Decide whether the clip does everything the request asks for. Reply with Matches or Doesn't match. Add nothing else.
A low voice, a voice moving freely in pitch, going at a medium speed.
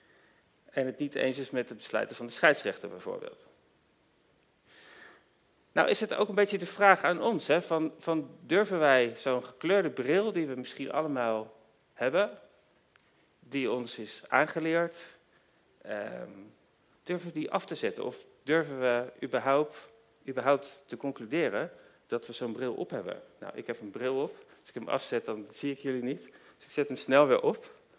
Doesn't match